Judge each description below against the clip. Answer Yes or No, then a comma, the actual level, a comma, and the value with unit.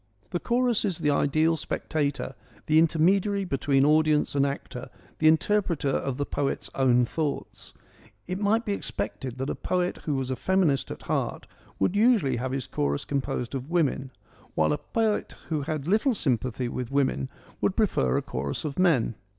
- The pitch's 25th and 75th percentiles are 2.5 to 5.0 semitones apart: No, wide, 5.5 semitones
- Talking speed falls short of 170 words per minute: No, average, 175 wpm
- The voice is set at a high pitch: No, medium, 145 Hz